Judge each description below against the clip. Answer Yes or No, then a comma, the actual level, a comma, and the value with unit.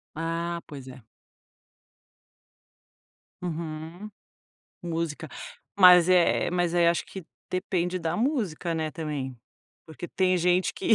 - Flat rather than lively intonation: Yes, narrow, 2.2 semitones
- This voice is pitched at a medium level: Yes, medium, 170 Hz